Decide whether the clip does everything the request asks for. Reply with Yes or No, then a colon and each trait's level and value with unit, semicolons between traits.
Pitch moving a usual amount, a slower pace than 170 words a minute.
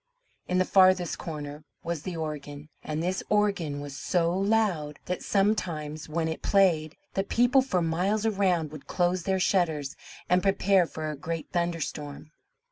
Yes: average, 3.8 semitones; average, 155 wpm